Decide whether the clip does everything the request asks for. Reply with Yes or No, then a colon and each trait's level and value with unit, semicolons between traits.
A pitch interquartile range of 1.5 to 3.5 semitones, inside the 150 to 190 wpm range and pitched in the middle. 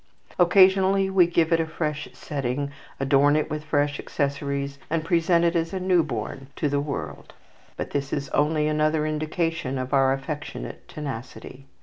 Yes: average, 2.9 semitones; average, 155 wpm; medium, 150 Hz